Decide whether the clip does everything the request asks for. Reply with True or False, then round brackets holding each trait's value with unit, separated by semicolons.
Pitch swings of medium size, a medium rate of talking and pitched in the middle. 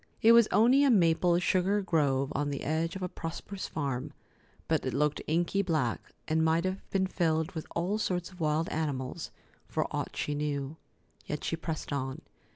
True (3.8 semitones; 180 wpm; 165 Hz)